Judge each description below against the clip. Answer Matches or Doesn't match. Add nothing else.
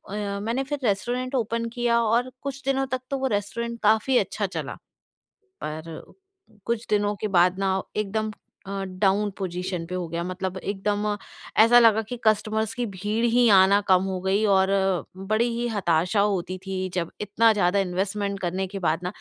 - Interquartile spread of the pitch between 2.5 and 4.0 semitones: Matches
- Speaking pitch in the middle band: Doesn't match